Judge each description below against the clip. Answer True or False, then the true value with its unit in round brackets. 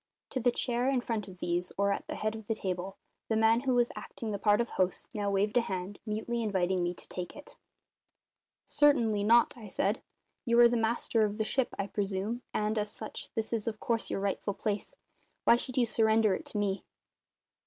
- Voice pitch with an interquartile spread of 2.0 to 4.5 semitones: True (2.8 semitones)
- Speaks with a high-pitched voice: True (215 Hz)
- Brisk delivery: True (215 wpm)